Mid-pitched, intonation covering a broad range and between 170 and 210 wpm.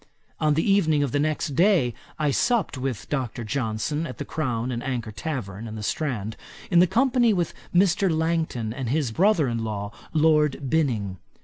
Yes: medium, 145 Hz; wide, 5.8 semitones; average, 175 wpm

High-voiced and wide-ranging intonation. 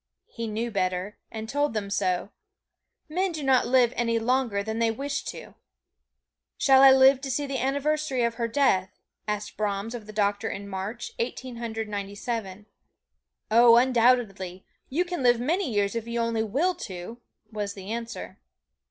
No: high, 230 Hz; average, 4.1 semitones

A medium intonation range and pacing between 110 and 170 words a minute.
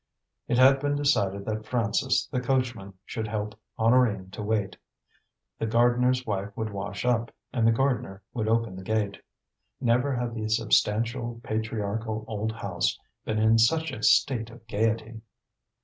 No: narrow, 2.2 semitones; average, 150 wpm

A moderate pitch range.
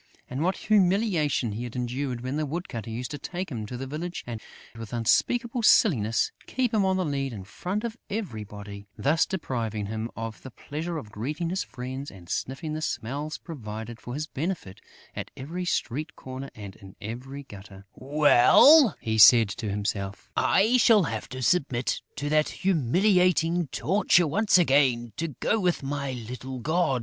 No: wide, 7.3 semitones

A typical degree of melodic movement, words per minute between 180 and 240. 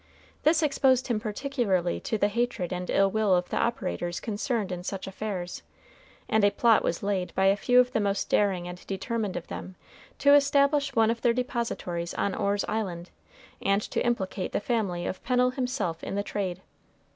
Yes: average, 4.6 semitones; average, 185 wpm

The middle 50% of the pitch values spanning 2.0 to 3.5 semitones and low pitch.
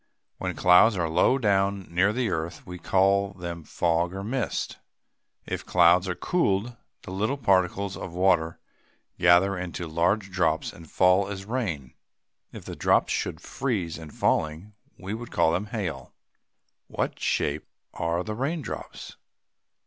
Yes: average, 3.2 semitones; very low, 95 Hz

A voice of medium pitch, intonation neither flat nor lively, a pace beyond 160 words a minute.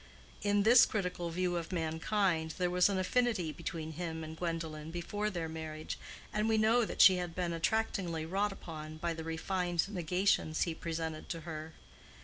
Yes: medium, 170 Hz; average, 3.1 semitones; average, 170 wpm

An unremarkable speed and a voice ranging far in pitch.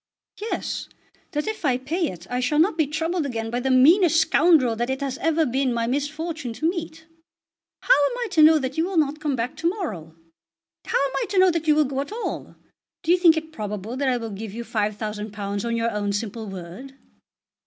No: fast, 220 wpm; wide, 5.9 semitones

